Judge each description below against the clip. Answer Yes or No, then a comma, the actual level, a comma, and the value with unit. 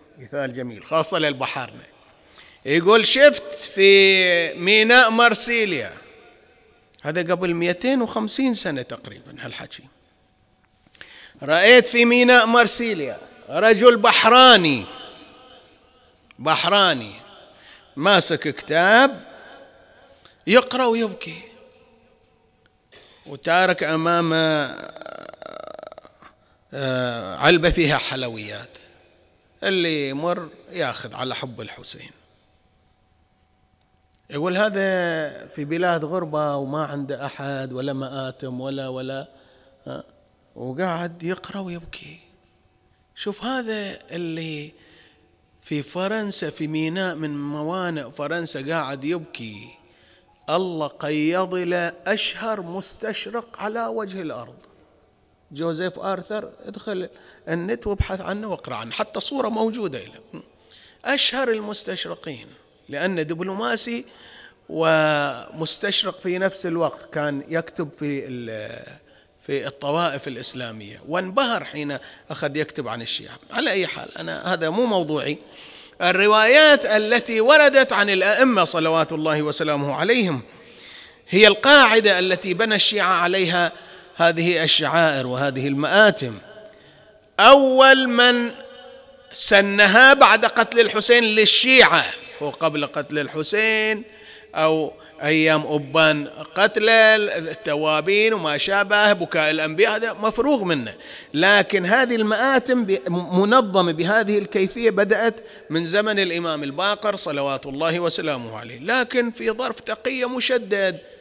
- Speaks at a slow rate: Yes, slow, 95 wpm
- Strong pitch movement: Yes, wide, 6.7 semitones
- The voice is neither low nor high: Yes, medium, 175 Hz